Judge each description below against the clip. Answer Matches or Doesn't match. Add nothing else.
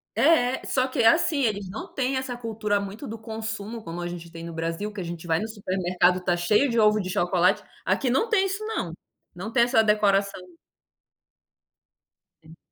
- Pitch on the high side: Matches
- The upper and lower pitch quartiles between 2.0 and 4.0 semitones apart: Doesn't match